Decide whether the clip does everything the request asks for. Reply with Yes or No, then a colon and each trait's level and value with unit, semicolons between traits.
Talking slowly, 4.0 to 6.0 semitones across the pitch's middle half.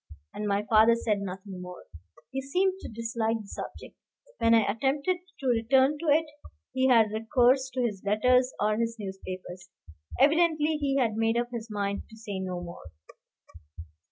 No: average, 165 wpm; average, 4.3 semitones